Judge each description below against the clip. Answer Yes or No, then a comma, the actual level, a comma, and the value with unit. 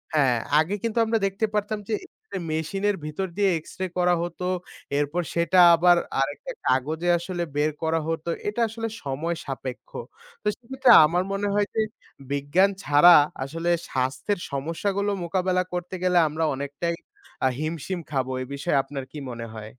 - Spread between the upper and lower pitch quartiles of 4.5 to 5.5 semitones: Yes, average, 5.1 semitones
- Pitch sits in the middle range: Yes, medium, 170 Hz